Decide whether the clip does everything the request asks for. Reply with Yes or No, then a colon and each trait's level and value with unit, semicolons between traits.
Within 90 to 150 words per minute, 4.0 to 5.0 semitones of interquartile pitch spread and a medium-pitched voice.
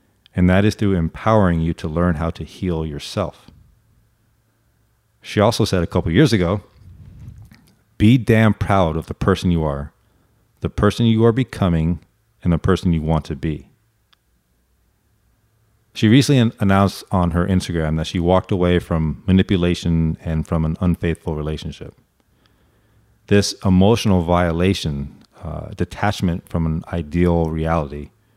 No: average, 140 wpm; average, 4.7 semitones; very low, 95 Hz